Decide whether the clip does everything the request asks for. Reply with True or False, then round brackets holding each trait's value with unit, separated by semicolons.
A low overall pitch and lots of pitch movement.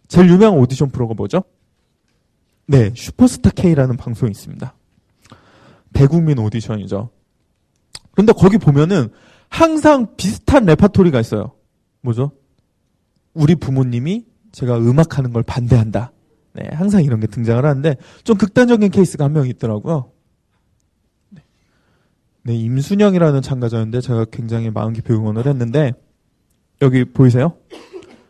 True (130 Hz; 6.4 semitones)